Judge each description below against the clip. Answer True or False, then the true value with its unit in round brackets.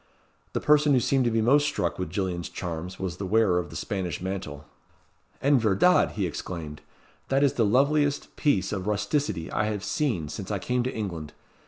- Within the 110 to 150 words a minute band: False (190 wpm)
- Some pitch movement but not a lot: False (6.2 semitones)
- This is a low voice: True (105 Hz)